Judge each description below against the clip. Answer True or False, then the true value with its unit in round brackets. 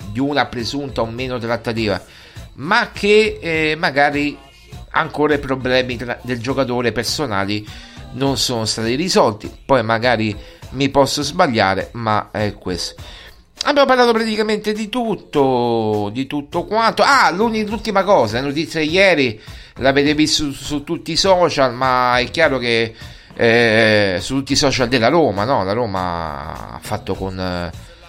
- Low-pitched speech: True (130 Hz)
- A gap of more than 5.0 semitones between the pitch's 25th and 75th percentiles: True (5.5 semitones)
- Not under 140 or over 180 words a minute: True (145 wpm)